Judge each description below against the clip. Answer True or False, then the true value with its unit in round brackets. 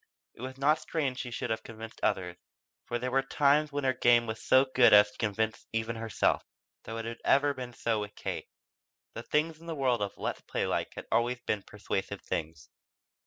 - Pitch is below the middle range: True (120 Hz)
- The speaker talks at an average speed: False (210 wpm)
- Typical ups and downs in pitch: True (3.3 semitones)